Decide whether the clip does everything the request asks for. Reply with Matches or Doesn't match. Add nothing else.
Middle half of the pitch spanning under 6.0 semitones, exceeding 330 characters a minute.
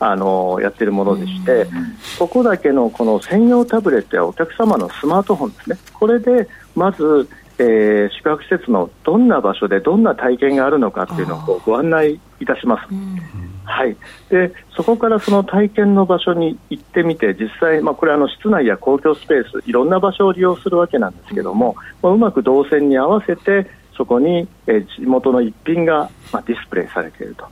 Doesn't match